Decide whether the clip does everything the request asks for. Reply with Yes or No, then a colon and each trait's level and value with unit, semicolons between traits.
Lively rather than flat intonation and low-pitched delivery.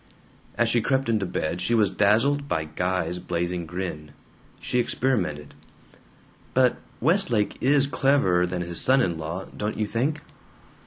Yes: wide, 6.7 semitones; low, 105 Hz